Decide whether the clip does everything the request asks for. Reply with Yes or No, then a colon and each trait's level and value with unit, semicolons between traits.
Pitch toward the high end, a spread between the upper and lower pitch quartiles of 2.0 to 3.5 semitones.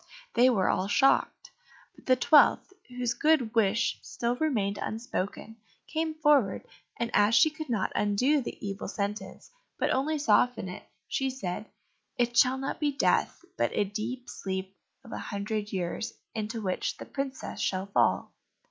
No: high, 235 Hz; average, 4.6 semitones